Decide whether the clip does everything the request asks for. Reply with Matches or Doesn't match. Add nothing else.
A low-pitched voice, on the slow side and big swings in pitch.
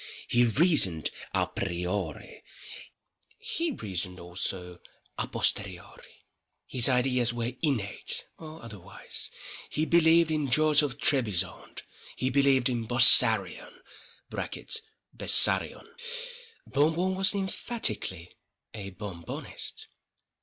Matches